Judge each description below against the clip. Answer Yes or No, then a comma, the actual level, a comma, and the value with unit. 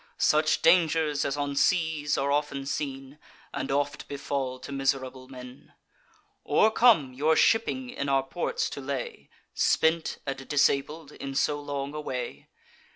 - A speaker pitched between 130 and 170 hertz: Yes, medium, 140 Hz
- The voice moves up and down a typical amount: No, narrow, 2.1 semitones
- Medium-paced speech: Yes, average, 145 wpm